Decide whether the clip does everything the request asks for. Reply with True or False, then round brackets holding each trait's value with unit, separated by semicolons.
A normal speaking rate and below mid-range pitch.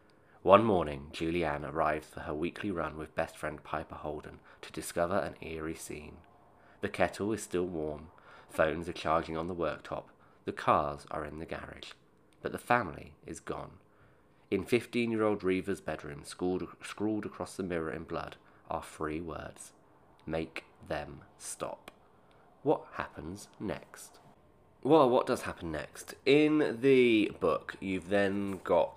True (150 wpm; 85 Hz)